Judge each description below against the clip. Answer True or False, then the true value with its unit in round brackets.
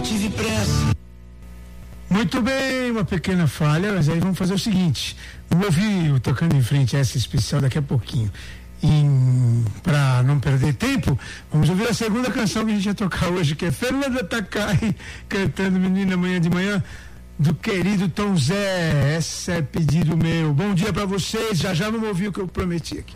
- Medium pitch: True (170 Hz)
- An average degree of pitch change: False (5.9 semitones)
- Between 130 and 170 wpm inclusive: False (185 wpm)